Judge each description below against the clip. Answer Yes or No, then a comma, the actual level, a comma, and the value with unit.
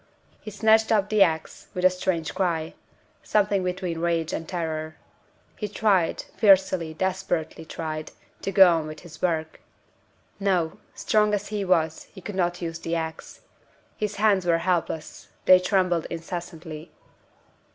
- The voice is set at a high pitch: No, medium, 180 Hz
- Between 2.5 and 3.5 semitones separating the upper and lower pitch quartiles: Yes, average, 3.1 semitones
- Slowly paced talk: No, average, 145 wpm